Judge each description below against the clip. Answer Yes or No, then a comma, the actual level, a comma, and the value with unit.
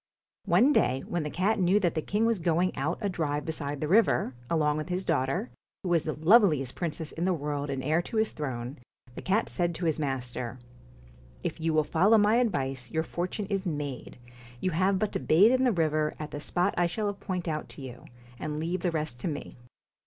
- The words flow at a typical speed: No, fast, 220 wpm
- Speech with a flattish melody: No, average, 4.2 semitones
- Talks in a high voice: No, medium, 165 Hz